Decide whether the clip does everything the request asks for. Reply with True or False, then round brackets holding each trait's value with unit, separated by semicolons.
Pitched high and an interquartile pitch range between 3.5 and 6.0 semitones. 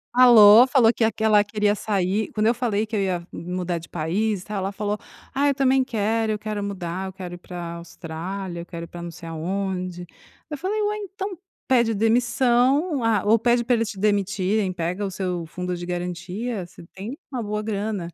True (205 Hz; 4.2 semitones)